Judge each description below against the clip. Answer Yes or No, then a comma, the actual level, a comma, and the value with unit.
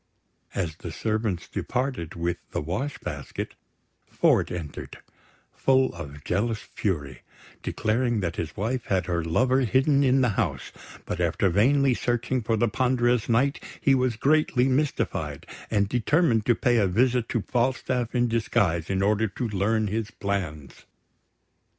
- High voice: No, low, 115 Hz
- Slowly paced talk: No, average, 145 wpm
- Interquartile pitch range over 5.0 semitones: Yes, wide, 5.4 semitones